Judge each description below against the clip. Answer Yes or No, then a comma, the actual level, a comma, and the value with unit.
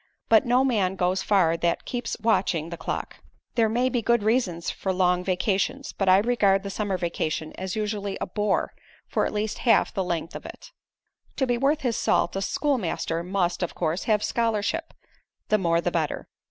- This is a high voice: Yes, high, 200 Hz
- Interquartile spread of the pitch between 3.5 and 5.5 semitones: Yes, average, 4.4 semitones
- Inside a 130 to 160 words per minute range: No, average, 190 wpm